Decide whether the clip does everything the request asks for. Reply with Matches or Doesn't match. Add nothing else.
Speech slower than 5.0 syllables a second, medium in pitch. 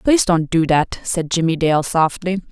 Matches